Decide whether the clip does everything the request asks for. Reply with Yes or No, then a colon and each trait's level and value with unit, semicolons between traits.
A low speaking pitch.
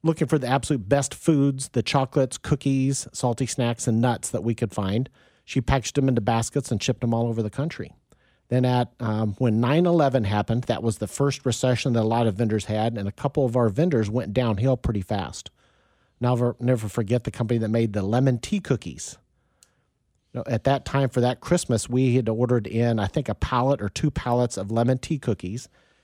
Yes: low, 125 Hz